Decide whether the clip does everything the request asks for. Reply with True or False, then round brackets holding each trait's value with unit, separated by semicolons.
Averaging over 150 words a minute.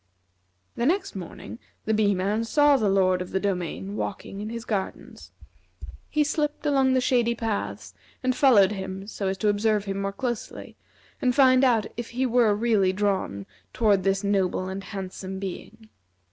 True (165 wpm)